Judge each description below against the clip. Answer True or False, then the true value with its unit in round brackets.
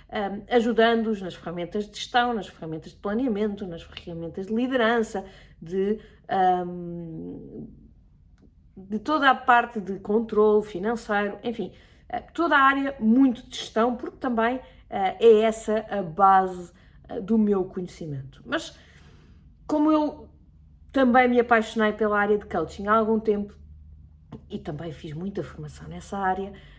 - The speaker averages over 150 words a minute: False (135 wpm)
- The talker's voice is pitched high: True (205 Hz)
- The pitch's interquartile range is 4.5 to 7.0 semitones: True (4.9 semitones)